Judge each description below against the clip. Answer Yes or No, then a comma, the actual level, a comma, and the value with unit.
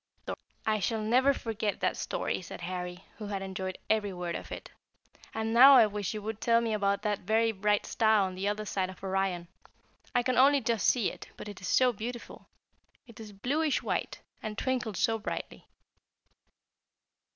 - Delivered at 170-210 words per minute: Yes, average, 185 wpm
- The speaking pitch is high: Yes, high, 215 Hz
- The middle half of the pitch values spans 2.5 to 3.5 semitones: Yes, average, 2.9 semitones